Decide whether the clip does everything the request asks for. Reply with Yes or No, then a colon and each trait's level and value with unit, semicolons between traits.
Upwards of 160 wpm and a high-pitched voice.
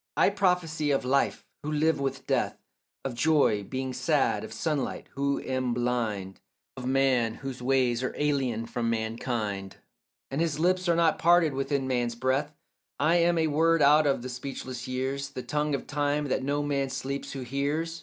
No: average, 175 wpm; low, 135 Hz